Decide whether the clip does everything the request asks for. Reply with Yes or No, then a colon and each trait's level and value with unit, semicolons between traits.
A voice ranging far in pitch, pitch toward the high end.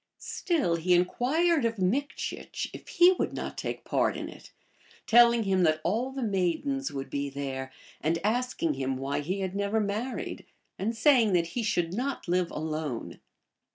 Yes: wide, 6.9 semitones; high, 195 Hz